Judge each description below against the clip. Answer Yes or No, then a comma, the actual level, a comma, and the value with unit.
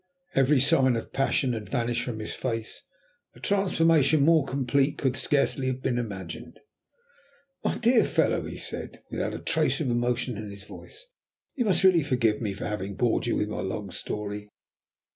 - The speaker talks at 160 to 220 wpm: Yes, average, 175 wpm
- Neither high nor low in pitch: No, low, 125 Hz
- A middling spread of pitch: Yes, average, 5.0 semitones